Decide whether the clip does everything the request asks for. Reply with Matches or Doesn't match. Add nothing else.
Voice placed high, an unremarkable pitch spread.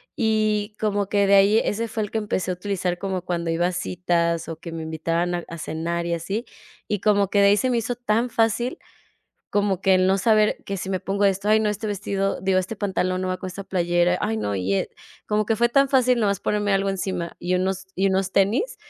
Matches